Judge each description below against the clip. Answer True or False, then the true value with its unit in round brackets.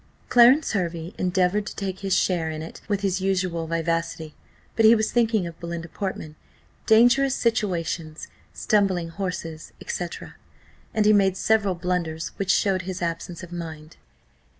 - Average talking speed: True (150 wpm)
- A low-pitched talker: False (185 Hz)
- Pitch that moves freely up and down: False (3.5 semitones)